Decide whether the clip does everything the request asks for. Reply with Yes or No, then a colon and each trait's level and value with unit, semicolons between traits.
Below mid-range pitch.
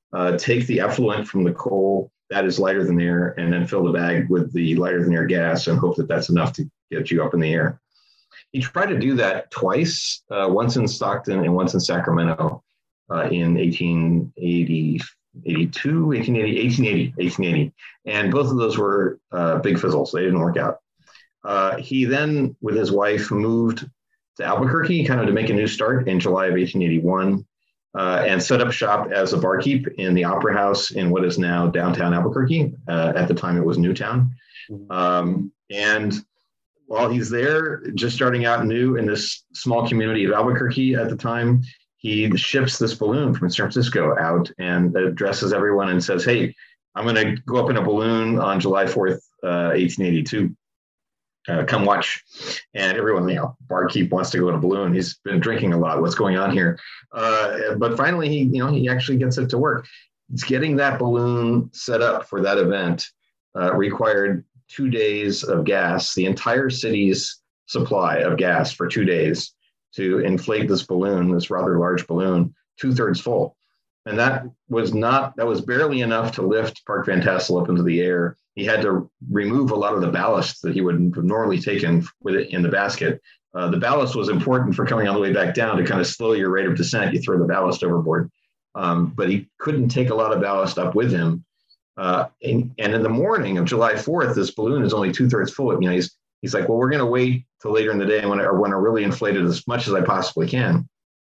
Yes: low, 105 Hz